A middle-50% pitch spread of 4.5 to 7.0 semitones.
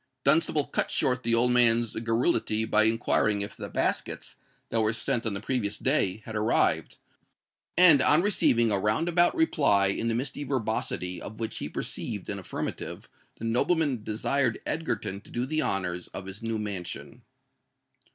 No: average, 4.0 semitones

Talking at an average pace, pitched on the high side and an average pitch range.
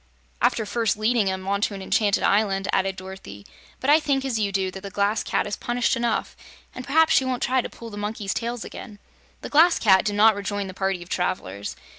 No: fast, 220 wpm; high, 205 Hz; average, 3.6 semitones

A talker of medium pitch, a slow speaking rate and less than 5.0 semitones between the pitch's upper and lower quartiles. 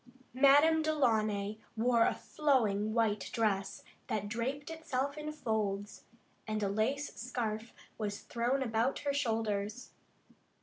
No: high, 230 Hz; slow, 120 wpm; average, 4.4 semitones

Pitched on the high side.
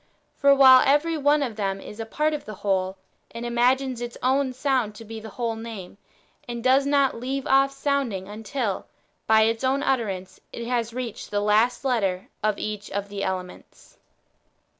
Yes: high, 235 Hz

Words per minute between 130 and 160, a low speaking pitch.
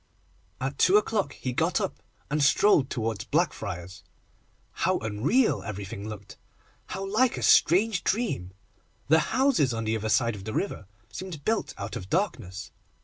Yes: average, 150 wpm; low, 130 Hz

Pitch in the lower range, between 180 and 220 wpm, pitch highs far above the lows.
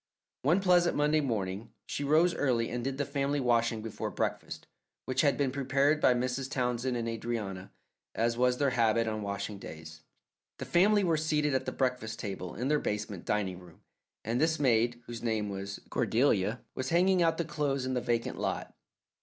No: low, 125 Hz; average, 185 wpm; average, 4.5 semitones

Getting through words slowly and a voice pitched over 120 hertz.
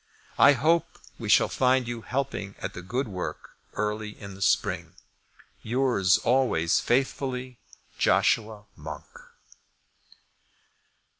No: slow, 105 wpm; low, 115 Hz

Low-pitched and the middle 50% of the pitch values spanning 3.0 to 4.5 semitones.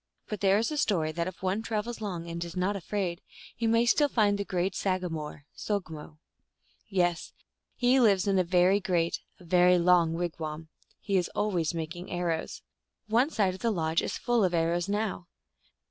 No: medium, 185 Hz; average, 3.5 semitones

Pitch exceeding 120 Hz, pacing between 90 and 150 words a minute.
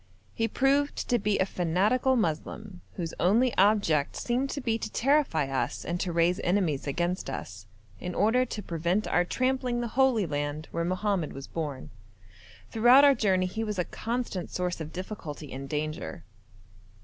No: medium, 185 Hz; average, 165 wpm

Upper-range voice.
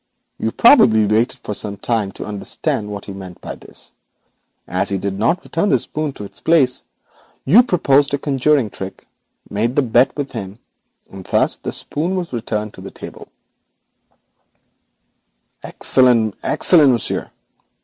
No: low, 120 Hz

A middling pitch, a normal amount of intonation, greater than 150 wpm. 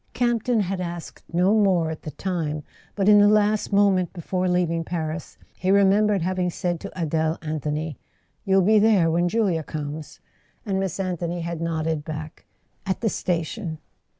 Yes: medium, 180 Hz; average, 3.5 semitones; average, 160 wpm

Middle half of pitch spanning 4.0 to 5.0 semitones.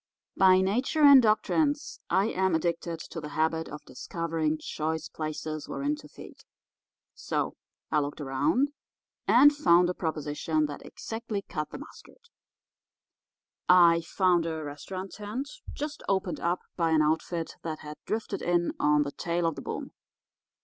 Yes: average, 4.7 semitones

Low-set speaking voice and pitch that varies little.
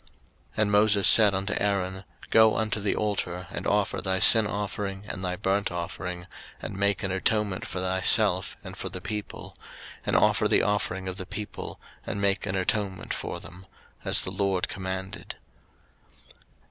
Yes: very low, 95 Hz; narrow, 1.7 semitones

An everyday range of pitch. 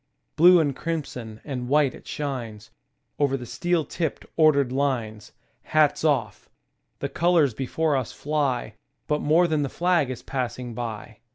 Yes: average, 4.1 semitones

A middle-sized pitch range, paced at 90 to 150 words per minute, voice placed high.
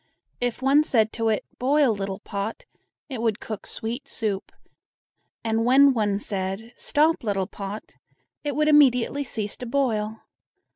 Yes: average, 4.4 semitones; average, 145 wpm; high, 225 Hz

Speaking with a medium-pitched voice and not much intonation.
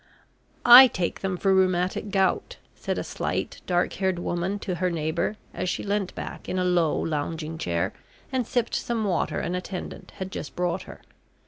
Yes: medium, 180 Hz; narrow, 2.3 semitones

